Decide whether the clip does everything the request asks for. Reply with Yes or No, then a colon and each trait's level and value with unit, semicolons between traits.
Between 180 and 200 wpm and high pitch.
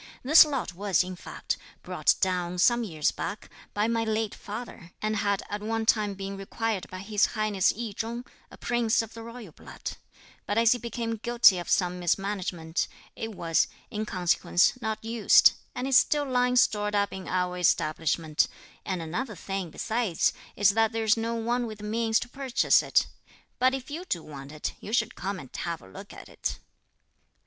Yes: average, 185 wpm; high, 210 Hz